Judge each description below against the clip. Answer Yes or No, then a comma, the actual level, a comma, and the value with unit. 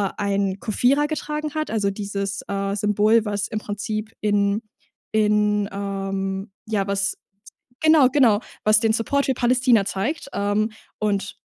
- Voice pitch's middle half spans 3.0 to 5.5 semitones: No, narrow, 2.4 semitones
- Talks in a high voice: Yes, high, 210 Hz